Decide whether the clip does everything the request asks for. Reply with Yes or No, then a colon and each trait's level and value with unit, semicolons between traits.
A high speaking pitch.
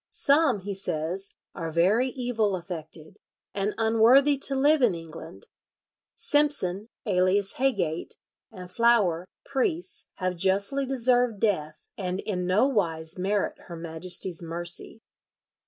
Yes: high, 195 Hz